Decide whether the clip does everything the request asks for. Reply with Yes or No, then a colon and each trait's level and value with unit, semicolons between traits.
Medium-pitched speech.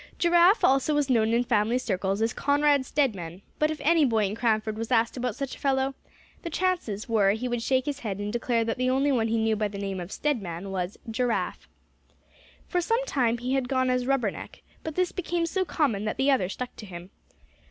No: high, 245 Hz